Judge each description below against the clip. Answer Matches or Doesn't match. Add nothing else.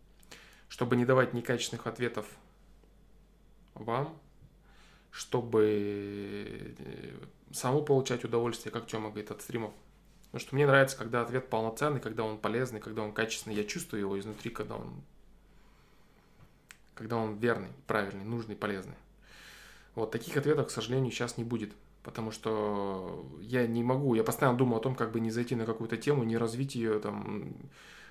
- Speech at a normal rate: Matches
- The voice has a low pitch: Matches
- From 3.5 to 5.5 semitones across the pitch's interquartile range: Doesn't match